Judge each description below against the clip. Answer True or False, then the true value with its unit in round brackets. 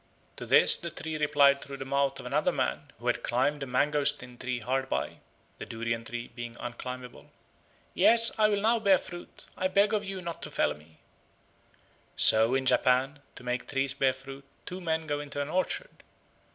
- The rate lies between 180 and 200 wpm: True (190 wpm)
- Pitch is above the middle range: False (140 Hz)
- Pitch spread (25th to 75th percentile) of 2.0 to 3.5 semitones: False (5.1 semitones)